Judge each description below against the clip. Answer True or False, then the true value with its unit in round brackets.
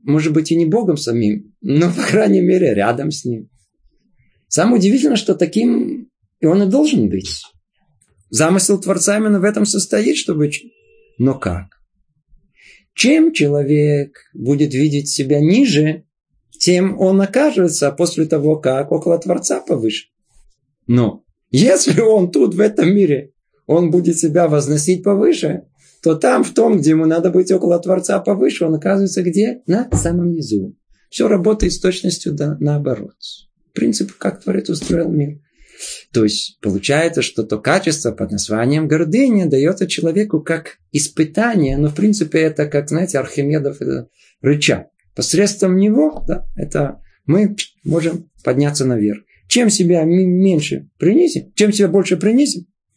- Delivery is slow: False (140 wpm)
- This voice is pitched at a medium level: True (165 Hz)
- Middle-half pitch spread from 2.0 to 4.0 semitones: False (5.2 semitones)